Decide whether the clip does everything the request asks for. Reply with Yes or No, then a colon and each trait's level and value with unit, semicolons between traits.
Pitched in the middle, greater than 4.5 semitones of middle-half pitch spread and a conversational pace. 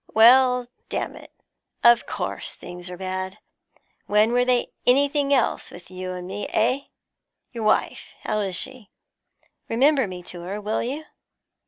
No: high, 220 Hz; average, 5.1 semitones; average, 150 wpm